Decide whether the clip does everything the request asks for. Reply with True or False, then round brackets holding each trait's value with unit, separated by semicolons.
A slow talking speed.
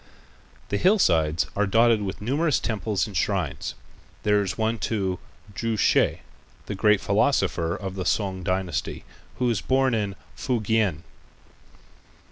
True (130 wpm)